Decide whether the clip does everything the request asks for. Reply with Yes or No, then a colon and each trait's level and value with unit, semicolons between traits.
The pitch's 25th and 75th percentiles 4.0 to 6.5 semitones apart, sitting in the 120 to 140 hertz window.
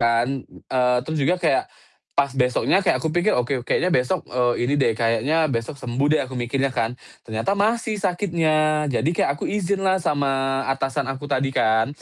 Yes: average, 4.6 semitones; low, 135 Hz